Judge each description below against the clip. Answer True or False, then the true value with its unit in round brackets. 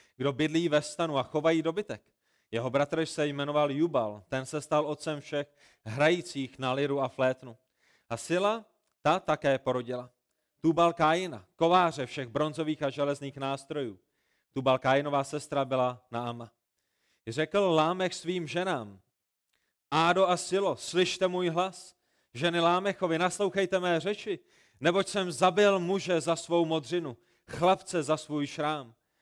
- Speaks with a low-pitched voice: False (155 Hz)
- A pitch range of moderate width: True (4.7 semitones)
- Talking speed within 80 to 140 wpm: True (135 wpm)